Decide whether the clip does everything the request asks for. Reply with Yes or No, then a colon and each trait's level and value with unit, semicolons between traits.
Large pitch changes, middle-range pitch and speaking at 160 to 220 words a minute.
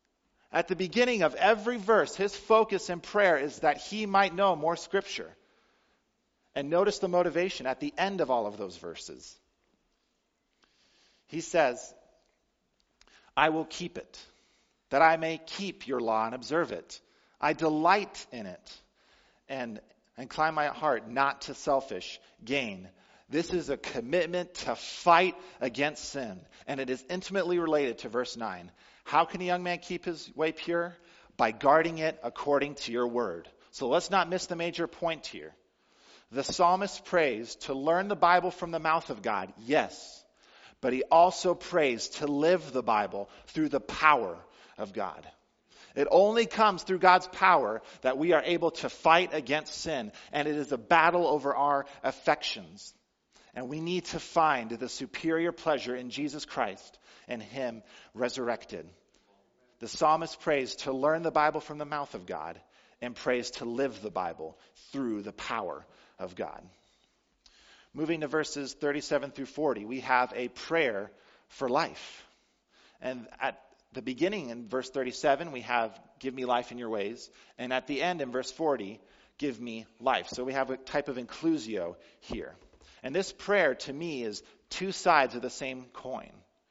No: average, 5.0 semitones; medium, 155 Hz; average, 165 wpm